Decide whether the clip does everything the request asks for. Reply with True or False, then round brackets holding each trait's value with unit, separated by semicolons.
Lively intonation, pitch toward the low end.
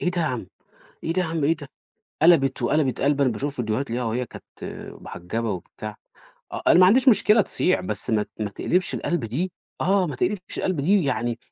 False (7.2 semitones; 145 Hz)